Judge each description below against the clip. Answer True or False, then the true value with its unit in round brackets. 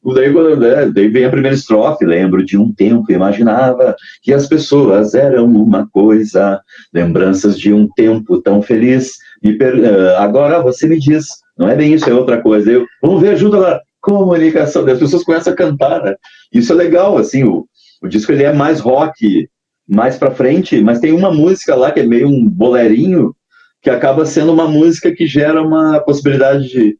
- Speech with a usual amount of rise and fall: False (6.2 semitones)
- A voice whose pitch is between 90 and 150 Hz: True (140 Hz)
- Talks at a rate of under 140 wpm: False (180 wpm)